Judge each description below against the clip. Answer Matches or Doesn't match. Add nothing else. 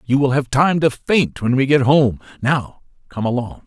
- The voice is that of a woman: Doesn't match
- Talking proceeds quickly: Matches